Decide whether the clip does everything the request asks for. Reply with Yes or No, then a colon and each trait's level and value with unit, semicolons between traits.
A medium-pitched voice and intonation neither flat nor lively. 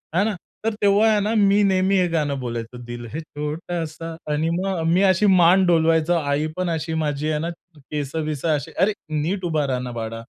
Yes: medium, 160 Hz; average, 4.2 semitones